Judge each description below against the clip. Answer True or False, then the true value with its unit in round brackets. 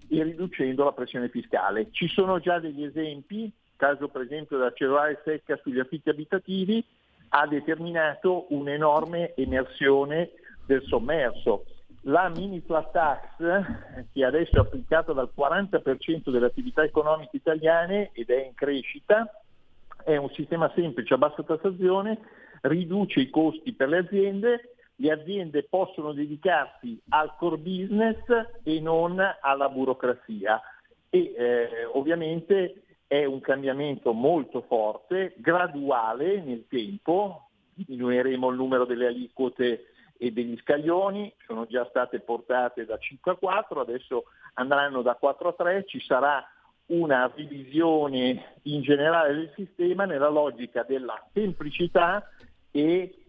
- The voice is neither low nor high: True (155 Hz)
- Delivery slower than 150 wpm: True (130 wpm)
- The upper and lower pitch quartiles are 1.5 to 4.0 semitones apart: False (5.5 semitones)